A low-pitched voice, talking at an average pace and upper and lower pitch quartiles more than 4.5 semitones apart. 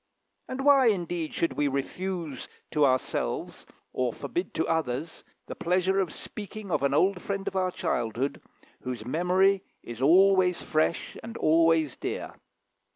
No: medium, 170 Hz; average, 145 wpm; average, 4.9 semitones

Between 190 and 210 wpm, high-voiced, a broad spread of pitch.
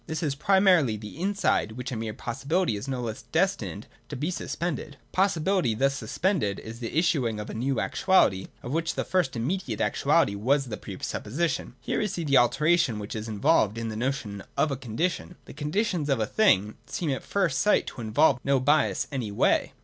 No: average, 200 wpm; low, 135 Hz; wide, 7.0 semitones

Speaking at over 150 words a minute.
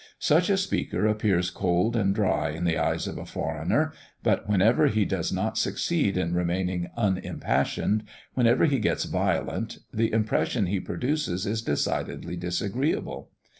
No: average, 145 wpm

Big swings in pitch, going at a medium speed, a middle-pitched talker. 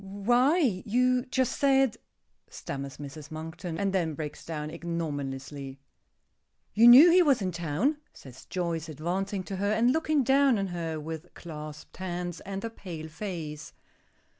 Yes: wide, 6.9 semitones; average, 150 wpm; medium, 180 Hz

